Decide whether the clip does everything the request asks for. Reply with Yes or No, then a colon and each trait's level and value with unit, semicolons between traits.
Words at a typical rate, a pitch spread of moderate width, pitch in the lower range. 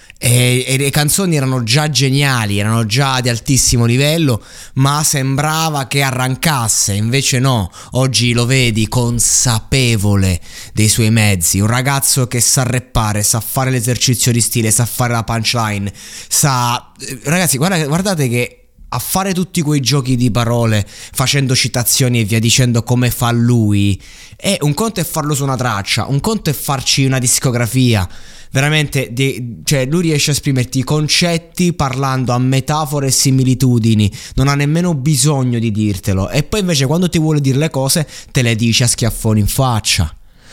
Yes: average, 160 wpm; average, 3.6 semitones; low, 130 Hz